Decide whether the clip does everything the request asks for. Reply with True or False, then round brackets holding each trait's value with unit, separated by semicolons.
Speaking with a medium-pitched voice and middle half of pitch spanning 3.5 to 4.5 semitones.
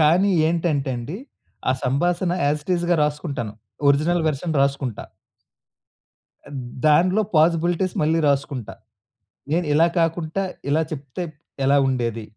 True (155 Hz; 3.8 semitones)